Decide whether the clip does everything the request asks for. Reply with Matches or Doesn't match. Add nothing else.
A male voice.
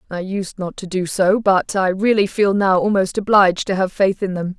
Doesn't match